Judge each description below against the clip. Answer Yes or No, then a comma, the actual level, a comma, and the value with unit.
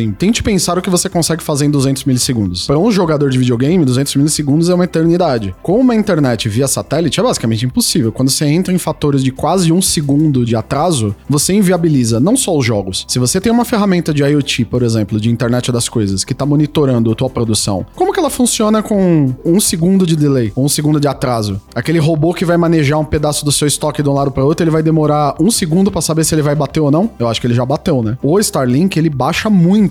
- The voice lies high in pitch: No, medium, 150 Hz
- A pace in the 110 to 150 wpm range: No, fast, 235 wpm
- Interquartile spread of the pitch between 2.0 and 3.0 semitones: No, wide, 5.6 semitones